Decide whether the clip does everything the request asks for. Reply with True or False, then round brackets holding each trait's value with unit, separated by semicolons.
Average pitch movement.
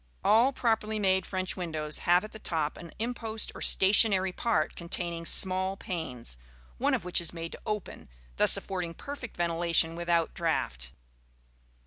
True (4.1 semitones)